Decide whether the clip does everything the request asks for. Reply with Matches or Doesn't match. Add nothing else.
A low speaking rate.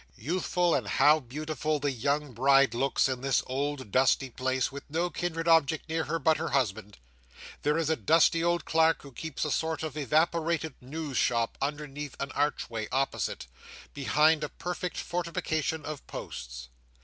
Doesn't match